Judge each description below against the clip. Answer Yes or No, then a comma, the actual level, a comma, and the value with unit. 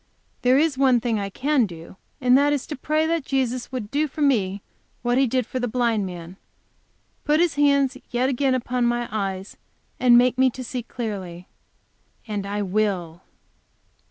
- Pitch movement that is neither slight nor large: Yes, average, 4.6 semitones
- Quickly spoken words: No, average, 180 wpm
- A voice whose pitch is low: No, high, 245 Hz